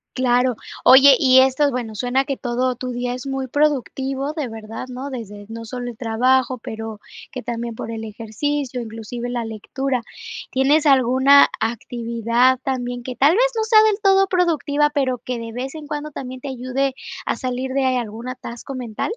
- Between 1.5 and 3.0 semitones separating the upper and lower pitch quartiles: Yes, narrow, 2.6 semitones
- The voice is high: Yes, very high, 255 Hz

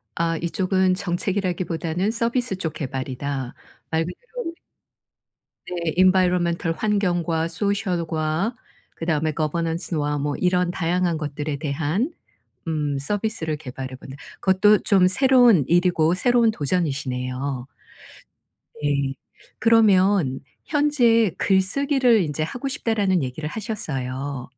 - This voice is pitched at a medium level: Yes, medium, 175 Hz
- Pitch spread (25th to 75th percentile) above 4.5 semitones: Yes, average, 5.2 semitones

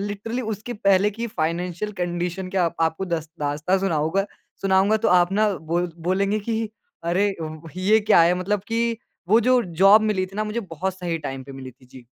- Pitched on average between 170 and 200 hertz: Yes, high, 190 Hz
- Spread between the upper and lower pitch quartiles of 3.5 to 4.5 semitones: Yes, average, 3.9 semitones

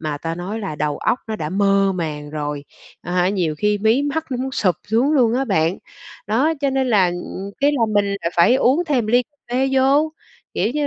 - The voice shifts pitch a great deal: Yes, wide, 7.1 semitones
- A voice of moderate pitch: No, high, 210 Hz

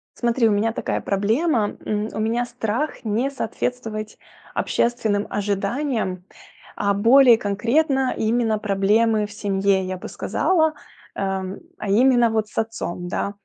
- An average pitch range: Yes, average, 3.0 semitones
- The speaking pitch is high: Yes, high, 220 Hz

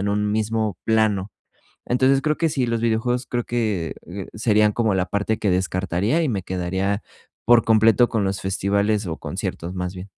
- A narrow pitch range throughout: No, average, 3.2 semitones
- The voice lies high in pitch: No, low, 105 Hz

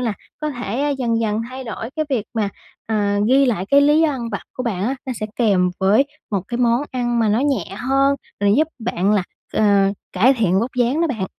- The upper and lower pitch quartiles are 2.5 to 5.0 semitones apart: Yes, average, 4.5 semitones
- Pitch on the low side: No, high, 235 Hz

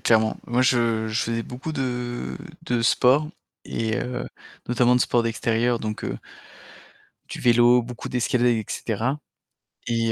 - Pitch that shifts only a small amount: Yes, narrow, 1.4 semitones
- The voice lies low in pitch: Yes, low, 120 Hz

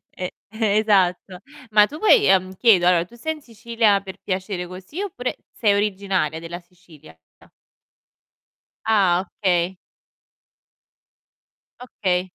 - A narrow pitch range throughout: No, average, 3.5 semitones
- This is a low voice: No, high, 190 Hz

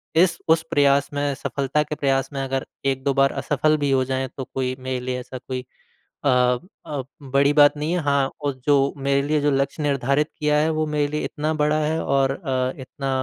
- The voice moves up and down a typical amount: No, narrow, 1.9 semitones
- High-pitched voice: No, medium, 140 Hz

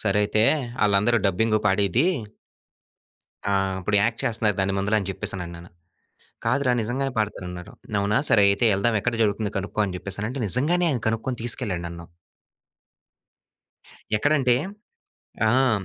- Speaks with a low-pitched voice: Yes, low, 105 Hz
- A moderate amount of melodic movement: Yes, average, 3.5 semitones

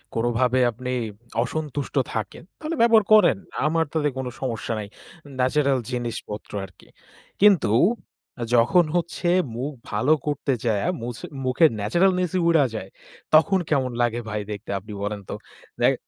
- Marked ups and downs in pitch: Yes, wide, 6.1 semitones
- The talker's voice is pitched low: Yes, low, 130 Hz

